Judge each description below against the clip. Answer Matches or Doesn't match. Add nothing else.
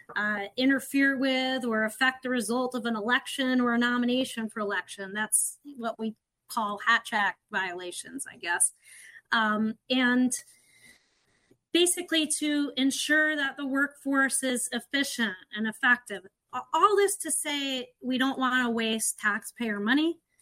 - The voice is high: Matches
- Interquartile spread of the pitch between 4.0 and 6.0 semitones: Doesn't match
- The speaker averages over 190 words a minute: Doesn't match